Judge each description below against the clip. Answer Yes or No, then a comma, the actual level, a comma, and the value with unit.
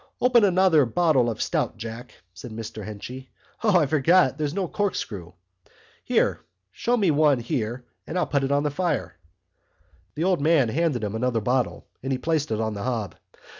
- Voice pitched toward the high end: No, low, 135 Hz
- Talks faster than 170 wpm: Yes, average, 180 wpm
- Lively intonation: Yes, wide, 6.6 semitones